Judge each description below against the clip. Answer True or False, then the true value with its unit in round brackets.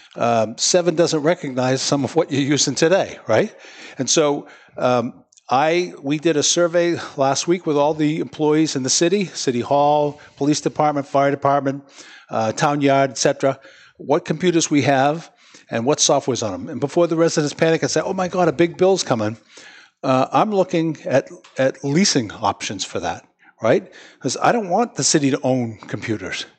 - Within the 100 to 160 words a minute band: False (180 wpm)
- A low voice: False (145 Hz)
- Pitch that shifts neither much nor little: True (3.5 semitones)